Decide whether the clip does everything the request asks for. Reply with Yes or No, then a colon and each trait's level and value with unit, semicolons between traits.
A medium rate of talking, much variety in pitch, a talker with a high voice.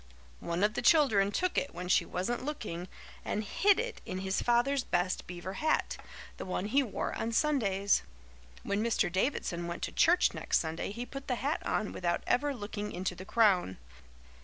Yes: average, 185 wpm; wide, 6.8 semitones; high, 210 Hz